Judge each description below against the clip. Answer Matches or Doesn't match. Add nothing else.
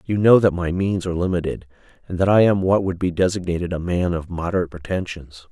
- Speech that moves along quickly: Matches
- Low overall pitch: Matches